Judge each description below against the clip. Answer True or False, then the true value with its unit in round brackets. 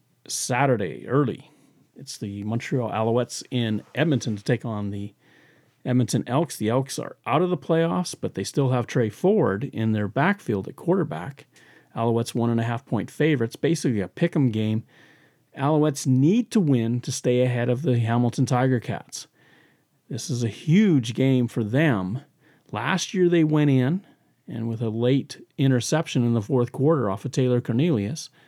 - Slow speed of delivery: False (170 wpm)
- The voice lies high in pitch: False (130 Hz)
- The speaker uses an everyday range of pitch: True (4.6 semitones)